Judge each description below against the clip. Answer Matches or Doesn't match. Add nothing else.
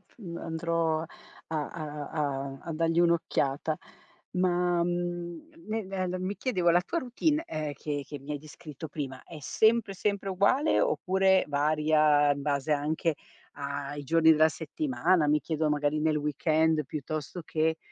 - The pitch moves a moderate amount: Matches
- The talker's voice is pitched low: Doesn't match